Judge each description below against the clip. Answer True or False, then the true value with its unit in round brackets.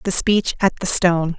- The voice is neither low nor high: True (180 Hz)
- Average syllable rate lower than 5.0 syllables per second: True (4.7 syllables/s)